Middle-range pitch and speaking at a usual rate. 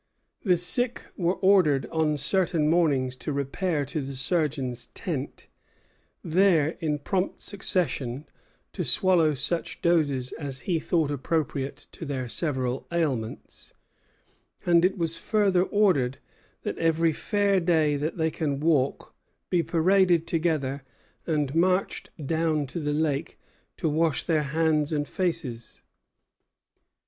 No: medium, 160 Hz; slow, 125 wpm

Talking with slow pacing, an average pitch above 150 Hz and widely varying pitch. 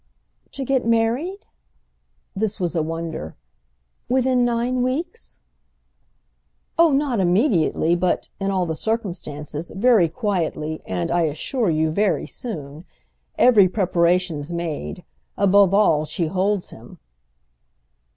Yes: slow, 100 wpm; medium, 185 Hz; wide, 6.6 semitones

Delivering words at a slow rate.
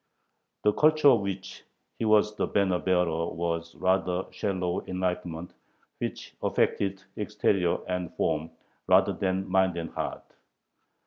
Yes: slow, 130 wpm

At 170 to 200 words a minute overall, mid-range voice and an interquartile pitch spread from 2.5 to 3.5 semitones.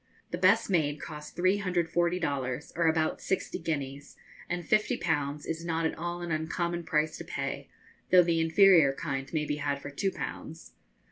Yes: average, 175 wpm; medium, 165 Hz; average, 2.8 semitones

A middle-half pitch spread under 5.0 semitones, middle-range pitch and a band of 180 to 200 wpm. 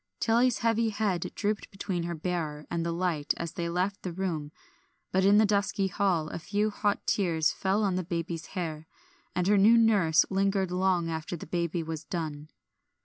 Yes: average, 3.4 semitones; medium, 180 Hz; average, 185 wpm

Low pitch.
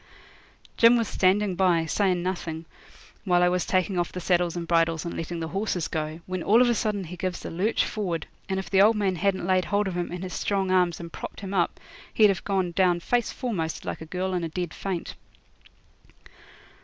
No: medium, 185 Hz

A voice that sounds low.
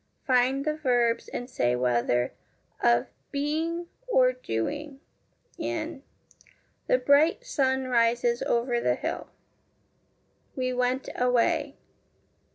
No: very high, 260 Hz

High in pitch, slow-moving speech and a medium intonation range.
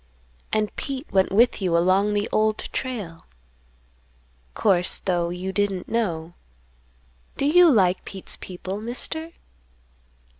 Yes: high, 200 Hz; slow, 115 wpm; average, 4.2 semitones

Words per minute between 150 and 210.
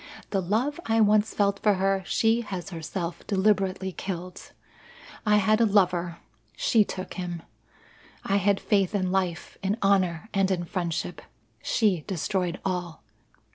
No: average, 140 wpm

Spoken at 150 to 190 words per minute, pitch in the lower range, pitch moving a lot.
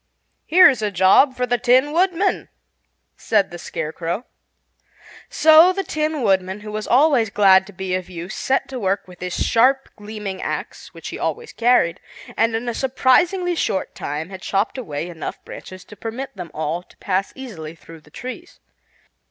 No: average, 170 wpm; high, 210 Hz; wide, 6.2 semitones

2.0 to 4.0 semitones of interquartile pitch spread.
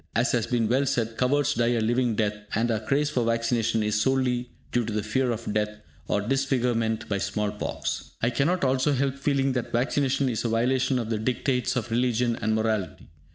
Yes: average, 2.8 semitones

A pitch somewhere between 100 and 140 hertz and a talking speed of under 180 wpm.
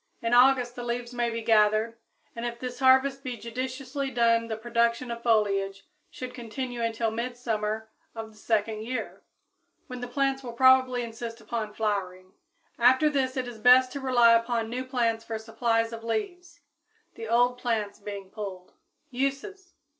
No: high, 235 Hz; average, 160 wpm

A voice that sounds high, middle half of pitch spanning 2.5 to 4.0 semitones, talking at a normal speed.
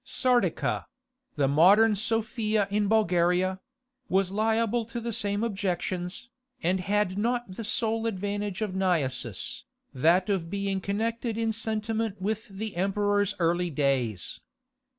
No: high, 205 Hz; average, 3.5 semitones; slow, 115 wpm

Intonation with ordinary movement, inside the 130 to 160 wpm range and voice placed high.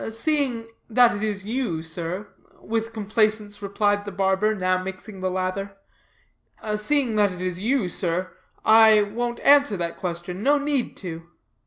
Yes: average, 3.5 semitones; average, 150 wpm; high, 205 Hz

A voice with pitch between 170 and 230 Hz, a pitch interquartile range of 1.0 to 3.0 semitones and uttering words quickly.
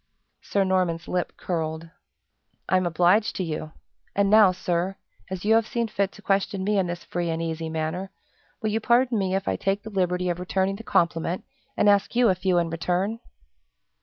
No: medium, 185 Hz; average, 2.7 semitones; average, 190 wpm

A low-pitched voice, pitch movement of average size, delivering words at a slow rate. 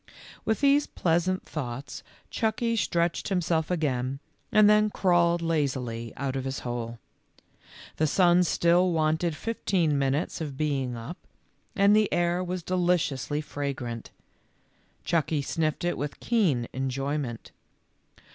No: medium, 160 Hz; average, 4.8 semitones; slow, 130 wpm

